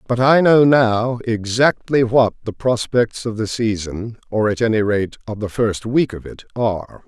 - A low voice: Yes, low, 115 Hz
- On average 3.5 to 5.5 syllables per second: Yes, 4.4 syllables/s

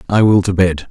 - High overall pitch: No, very low, 95 Hz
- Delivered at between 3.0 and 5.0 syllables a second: No, 5.6 syllables/s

